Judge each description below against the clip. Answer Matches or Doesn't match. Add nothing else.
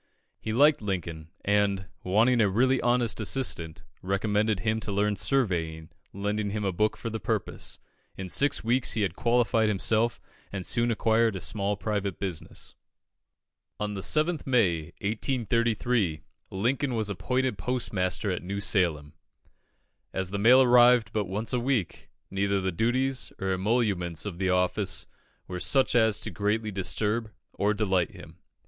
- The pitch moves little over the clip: Doesn't match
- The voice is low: Matches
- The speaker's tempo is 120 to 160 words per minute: Matches